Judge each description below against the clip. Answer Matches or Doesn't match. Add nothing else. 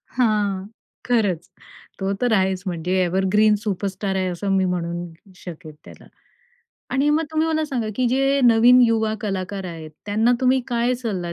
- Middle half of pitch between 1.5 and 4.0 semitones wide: Doesn't match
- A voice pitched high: Matches